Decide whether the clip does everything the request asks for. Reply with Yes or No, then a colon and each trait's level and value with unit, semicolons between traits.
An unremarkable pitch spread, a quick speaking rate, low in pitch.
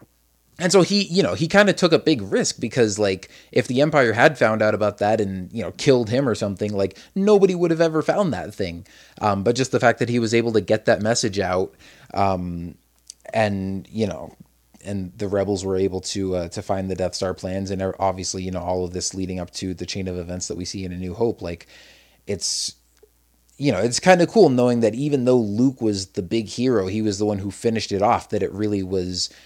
Yes: average, 4.4 semitones; fast, 240 wpm; low, 100 Hz